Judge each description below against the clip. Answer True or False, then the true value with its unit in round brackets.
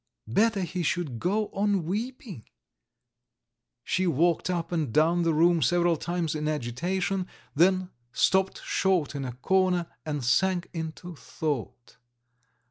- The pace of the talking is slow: True (125 wpm)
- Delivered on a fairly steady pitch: False (3.5 semitones)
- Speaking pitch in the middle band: True (175 Hz)